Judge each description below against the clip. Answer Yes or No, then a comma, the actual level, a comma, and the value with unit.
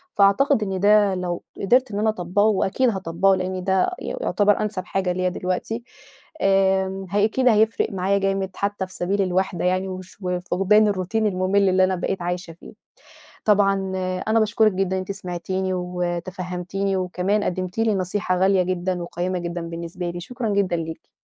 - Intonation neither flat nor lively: No, narrow, 1.9 semitones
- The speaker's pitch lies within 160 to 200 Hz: Yes, high, 190 Hz